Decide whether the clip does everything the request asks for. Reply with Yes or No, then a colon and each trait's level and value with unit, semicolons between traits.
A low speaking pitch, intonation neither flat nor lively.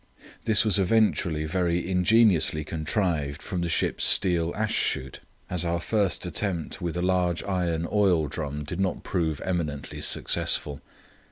Yes: very low, 85 Hz; average, 3.2 semitones